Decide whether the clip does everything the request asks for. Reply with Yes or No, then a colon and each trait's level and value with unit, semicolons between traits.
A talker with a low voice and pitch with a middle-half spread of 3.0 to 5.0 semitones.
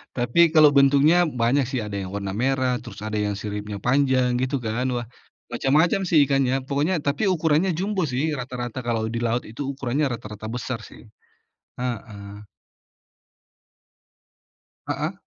Yes: low, 125 Hz; average, 3.7 semitones